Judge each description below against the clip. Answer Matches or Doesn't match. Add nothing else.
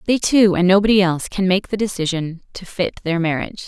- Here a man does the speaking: Doesn't match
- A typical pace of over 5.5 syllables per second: Matches